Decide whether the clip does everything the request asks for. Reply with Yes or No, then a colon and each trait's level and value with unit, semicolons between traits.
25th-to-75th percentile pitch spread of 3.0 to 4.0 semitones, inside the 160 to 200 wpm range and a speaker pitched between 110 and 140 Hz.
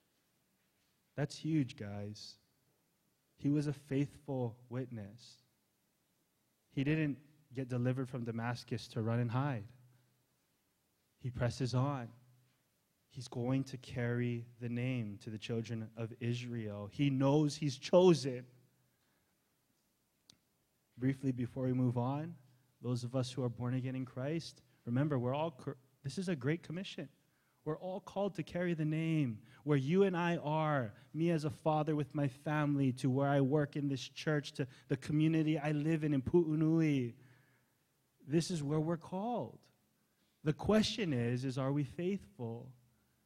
No: average, 3.6 semitones; average, 145 wpm; low, 135 Hz